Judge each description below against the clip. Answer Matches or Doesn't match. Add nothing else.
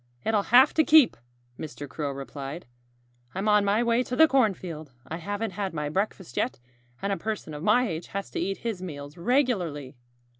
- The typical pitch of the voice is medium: Doesn't match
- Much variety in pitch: Matches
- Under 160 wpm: Doesn't match